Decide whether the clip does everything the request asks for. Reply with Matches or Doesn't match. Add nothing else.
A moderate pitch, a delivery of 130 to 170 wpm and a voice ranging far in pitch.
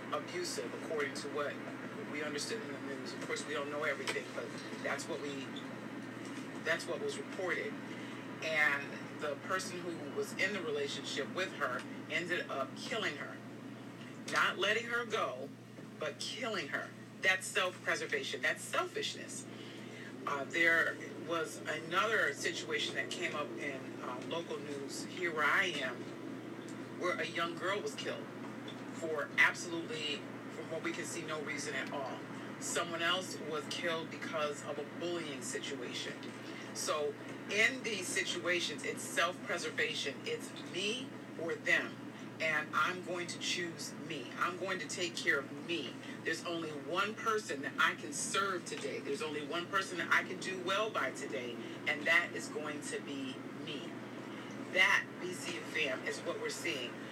Matches